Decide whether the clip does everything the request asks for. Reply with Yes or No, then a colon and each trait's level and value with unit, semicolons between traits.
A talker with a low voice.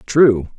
Yes: low, 120 Hz